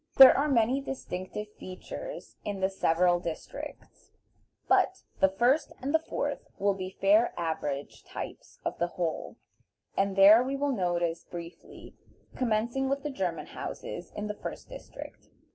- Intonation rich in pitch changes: Yes, wide, 6.7 semitones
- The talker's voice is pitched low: No, high, 200 Hz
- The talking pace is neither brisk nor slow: Yes, average, 145 wpm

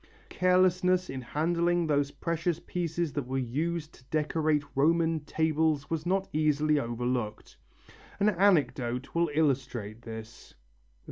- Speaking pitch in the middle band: Yes, medium, 155 Hz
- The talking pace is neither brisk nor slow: No, slow, 120 wpm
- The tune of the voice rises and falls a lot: No, average, 4.1 semitones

